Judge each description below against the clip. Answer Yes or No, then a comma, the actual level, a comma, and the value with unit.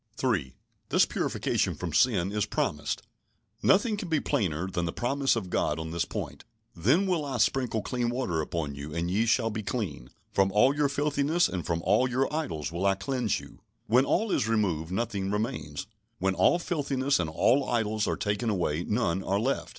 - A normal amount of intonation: No, wide, 7.2 semitones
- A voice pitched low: Yes, low, 105 Hz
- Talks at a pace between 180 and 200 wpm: Yes, average, 190 wpm